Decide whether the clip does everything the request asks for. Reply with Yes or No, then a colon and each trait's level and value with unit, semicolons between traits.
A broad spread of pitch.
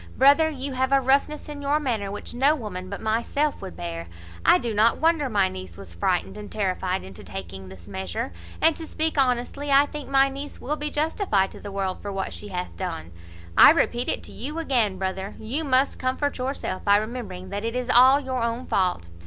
Yes: wide, 6.8 semitones